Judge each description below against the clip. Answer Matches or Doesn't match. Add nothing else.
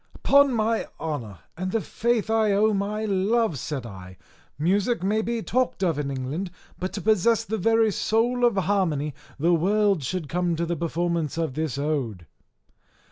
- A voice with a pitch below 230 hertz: Matches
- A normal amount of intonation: Doesn't match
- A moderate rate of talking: Matches